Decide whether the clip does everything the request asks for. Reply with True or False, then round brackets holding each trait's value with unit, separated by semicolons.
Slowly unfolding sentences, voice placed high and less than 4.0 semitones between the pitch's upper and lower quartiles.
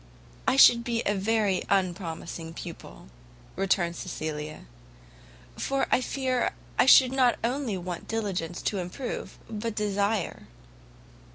False (115 wpm; 200 Hz; 5.1 semitones)